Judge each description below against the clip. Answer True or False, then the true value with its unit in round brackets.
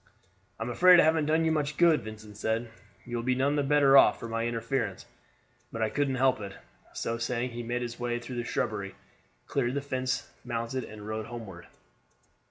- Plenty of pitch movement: False (3.1 semitones)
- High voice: False (120 Hz)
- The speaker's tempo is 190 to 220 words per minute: True (200 wpm)